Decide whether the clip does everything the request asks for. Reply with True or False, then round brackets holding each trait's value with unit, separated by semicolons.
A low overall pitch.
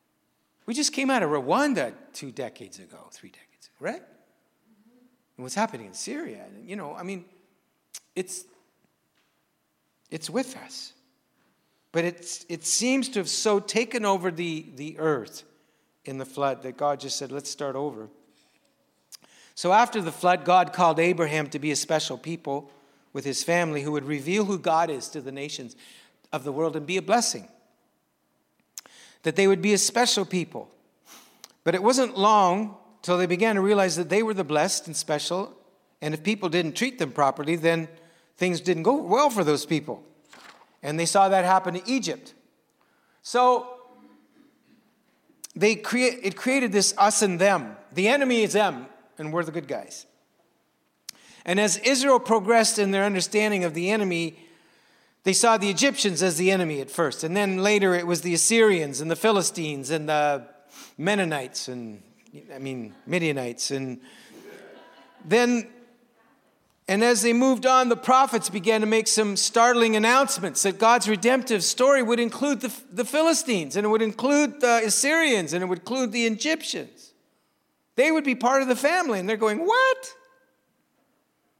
False (195 Hz)